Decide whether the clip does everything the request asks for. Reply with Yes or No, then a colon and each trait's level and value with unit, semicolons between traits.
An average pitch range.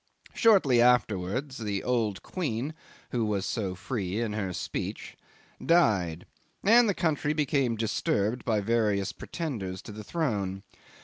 No: wide, 5.8 semitones